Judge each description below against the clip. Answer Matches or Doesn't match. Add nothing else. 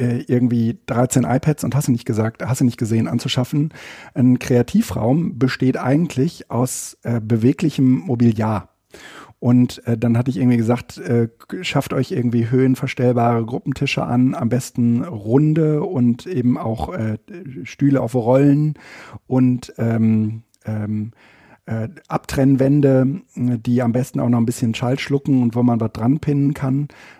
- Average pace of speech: Matches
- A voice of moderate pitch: Doesn't match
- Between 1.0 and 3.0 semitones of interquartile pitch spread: Matches